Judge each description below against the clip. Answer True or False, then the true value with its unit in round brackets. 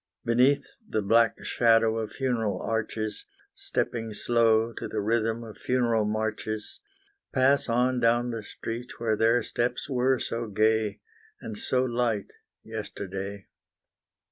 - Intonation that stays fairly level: True (1.9 semitones)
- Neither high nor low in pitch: False (115 Hz)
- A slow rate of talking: True (125 wpm)